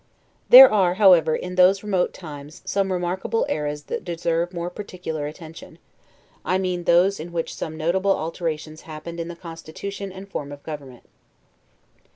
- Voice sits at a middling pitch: Yes, medium, 170 Hz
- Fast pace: No, average, 155 wpm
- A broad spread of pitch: No, average, 3.1 semitones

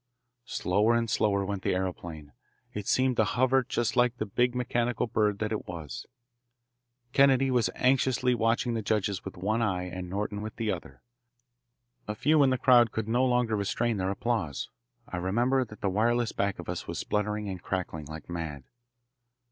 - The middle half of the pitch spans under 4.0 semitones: No, average, 4.3 semitones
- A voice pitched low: Yes, low, 105 Hz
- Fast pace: No, average, 180 wpm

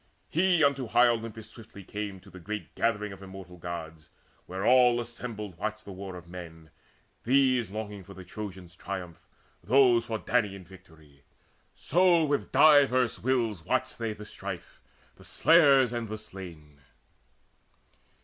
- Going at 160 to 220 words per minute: No, average, 145 wpm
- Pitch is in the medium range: No, low, 105 Hz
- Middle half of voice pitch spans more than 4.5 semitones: Yes, average, 5.1 semitones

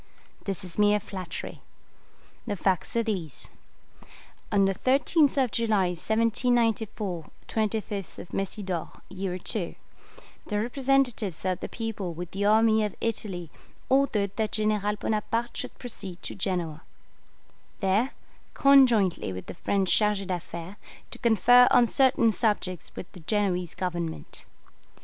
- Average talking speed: No, slow, 125 wpm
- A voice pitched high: Yes, high, 205 Hz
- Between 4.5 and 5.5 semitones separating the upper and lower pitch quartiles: No, average, 3.7 semitones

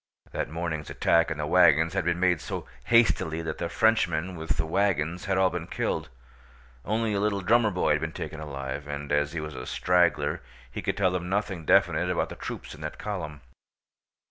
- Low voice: Yes, very low, 85 Hz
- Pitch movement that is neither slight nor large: Yes, average, 3.7 semitones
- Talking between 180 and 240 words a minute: Yes, average, 200 wpm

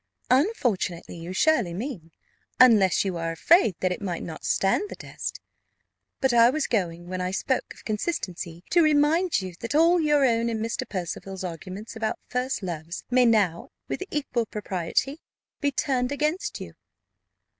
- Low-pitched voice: No, high, 225 Hz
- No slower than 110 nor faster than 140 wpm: No, average, 160 wpm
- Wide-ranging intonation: Yes, wide, 7.5 semitones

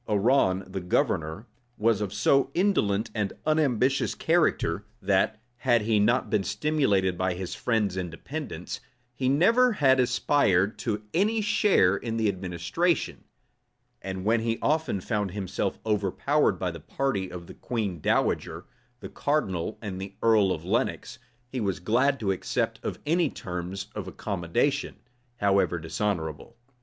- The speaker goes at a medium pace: Yes, average, 145 wpm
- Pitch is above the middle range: No, low, 105 Hz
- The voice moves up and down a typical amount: No, wide, 6.1 semitones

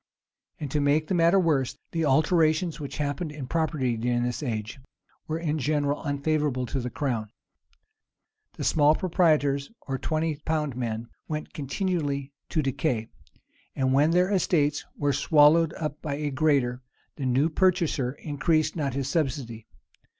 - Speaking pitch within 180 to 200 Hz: No, medium, 145 Hz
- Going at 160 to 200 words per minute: No, average, 150 wpm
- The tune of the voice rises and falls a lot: No, average, 2.9 semitones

